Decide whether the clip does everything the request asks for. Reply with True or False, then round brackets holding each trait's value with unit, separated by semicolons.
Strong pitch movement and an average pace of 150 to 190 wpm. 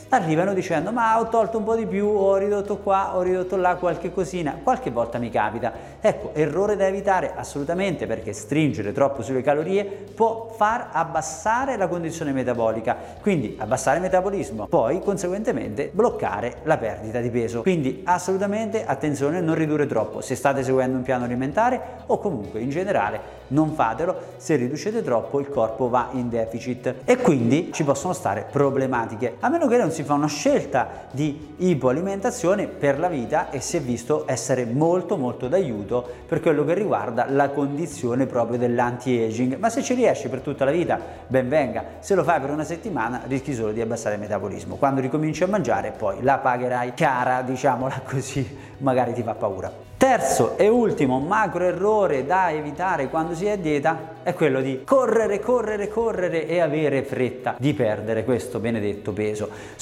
True (6.8 semitones; 170 wpm)